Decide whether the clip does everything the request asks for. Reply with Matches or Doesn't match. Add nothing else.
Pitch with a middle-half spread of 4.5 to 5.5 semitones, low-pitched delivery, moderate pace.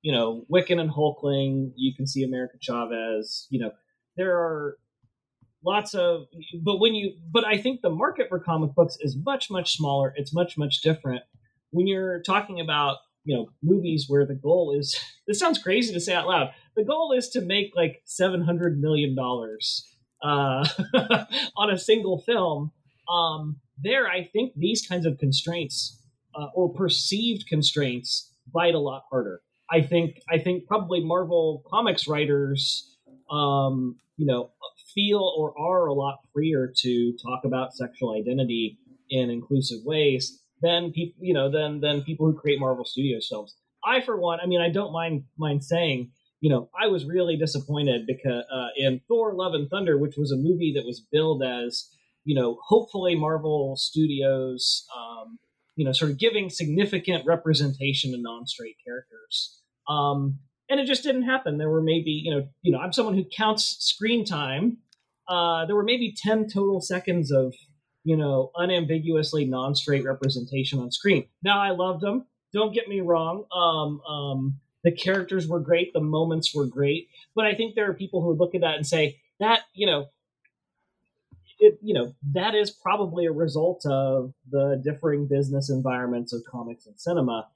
Doesn't match